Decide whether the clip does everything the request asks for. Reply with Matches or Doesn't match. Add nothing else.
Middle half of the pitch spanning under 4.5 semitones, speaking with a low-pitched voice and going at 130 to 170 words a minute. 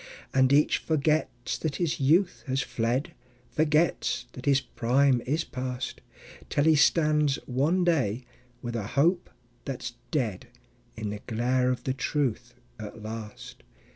Matches